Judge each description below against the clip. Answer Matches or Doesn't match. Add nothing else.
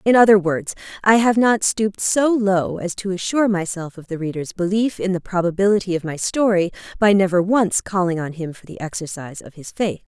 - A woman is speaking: Matches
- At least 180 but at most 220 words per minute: Matches